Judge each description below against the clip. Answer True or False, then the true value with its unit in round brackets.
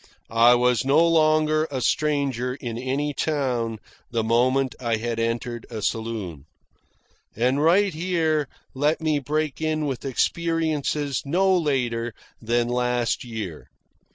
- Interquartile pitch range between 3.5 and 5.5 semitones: True (4.6 semitones)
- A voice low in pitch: True (130 Hz)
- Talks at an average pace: False (125 wpm)